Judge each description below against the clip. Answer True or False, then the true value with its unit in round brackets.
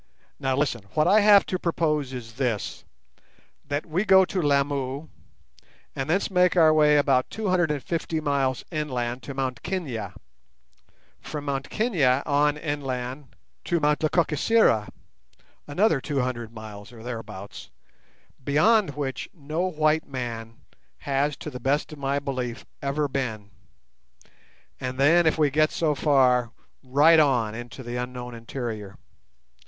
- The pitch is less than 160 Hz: True (140 Hz)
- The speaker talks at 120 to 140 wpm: True (135 wpm)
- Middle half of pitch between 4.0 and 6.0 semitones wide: False (3.6 semitones)